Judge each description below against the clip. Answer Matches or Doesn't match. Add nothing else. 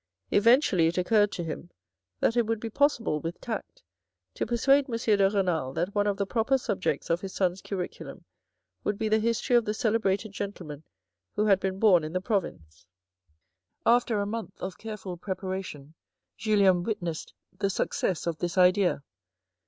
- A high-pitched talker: Matches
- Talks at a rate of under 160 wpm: Doesn't match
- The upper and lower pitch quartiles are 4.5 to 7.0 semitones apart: Doesn't match